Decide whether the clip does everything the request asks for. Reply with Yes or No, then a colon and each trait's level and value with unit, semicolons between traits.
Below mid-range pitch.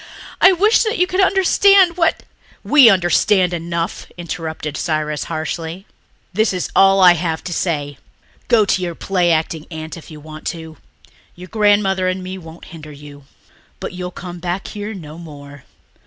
No: medium, 175 Hz